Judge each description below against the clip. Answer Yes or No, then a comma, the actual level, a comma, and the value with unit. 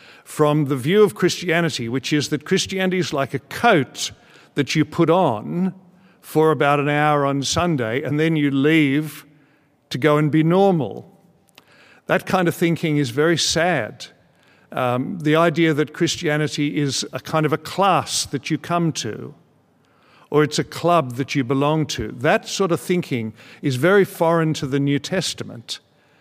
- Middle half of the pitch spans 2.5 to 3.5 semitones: Yes, average, 2.9 semitones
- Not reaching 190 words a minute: Yes, average, 165 wpm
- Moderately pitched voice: Yes, medium, 150 Hz